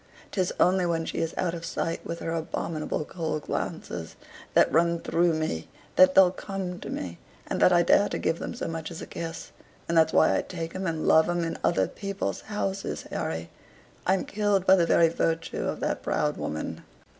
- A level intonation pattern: Yes, narrow, 2.3 semitones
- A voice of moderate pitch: Yes, medium, 170 Hz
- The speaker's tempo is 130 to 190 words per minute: No, average, 200 wpm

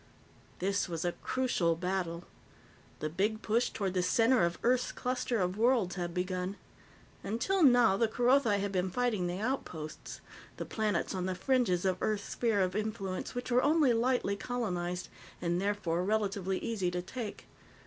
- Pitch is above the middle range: Yes, high, 200 Hz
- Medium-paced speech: Yes, average, 160 wpm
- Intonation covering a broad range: No, average, 4.8 semitones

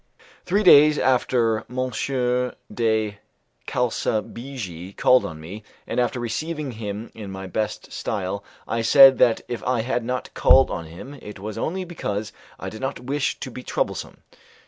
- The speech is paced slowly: No, average, 155 wpm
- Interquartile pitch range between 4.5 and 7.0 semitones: No, average, 3.8 semitones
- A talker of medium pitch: No, low, 115 Hz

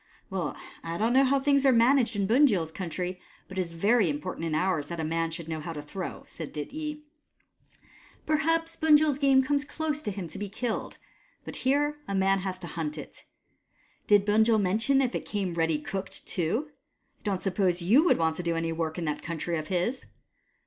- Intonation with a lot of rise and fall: Yes, wide, 8.0 semitones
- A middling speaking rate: No, fast, 210 wpm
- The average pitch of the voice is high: Yes, high, 195 Hz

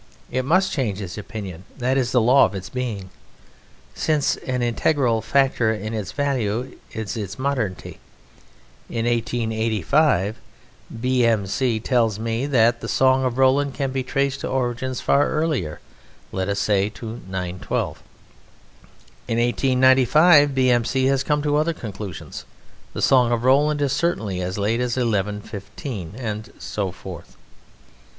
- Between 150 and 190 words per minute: No, average, 140 wpm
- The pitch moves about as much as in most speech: Yes, average, 3.9 semitones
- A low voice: Yes, low, 120 Hz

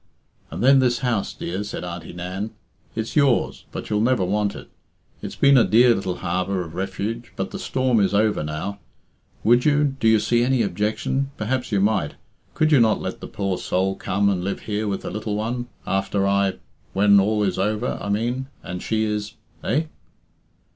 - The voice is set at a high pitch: No, low, 105 Hz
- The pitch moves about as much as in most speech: Yes, average, 3.7 semitones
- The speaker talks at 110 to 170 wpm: No, average, 190 wpm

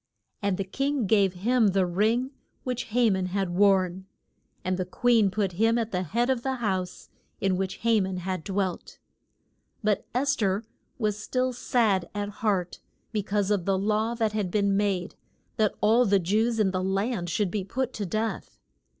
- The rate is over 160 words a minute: Yes, average, 185 wpm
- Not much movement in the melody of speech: No, average, 3.3 semitones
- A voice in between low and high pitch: No, high, 205 Hz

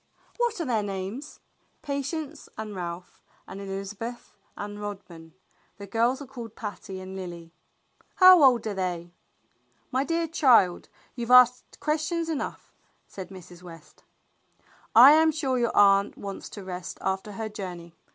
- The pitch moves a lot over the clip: Yes, wide, 6.1 semitones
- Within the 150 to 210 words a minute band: No, average, 140 wpm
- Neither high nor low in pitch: No, high, 210 Hz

